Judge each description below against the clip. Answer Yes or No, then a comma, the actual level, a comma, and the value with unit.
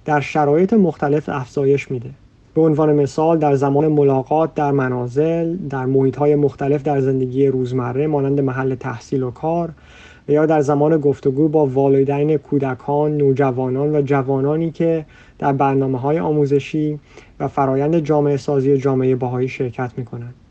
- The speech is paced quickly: No, average, 145 wpm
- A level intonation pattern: Yes, narrow, 2.1 semitones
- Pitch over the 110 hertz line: Yes, medium, 140 Hz